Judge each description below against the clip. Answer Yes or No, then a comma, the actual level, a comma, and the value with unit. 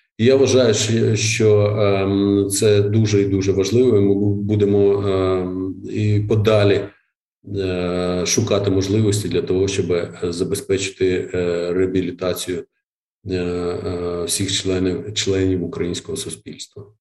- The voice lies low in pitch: Yes, low, 100 Hz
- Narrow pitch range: Yes, narrow, 2.1 semitones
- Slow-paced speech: Yes, slow, 90 wpm